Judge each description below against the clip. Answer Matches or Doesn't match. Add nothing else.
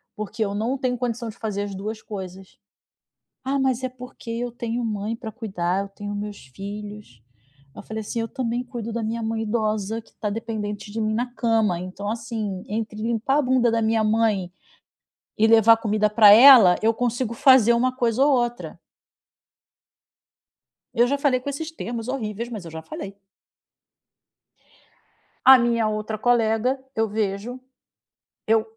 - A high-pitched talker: Matches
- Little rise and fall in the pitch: Matches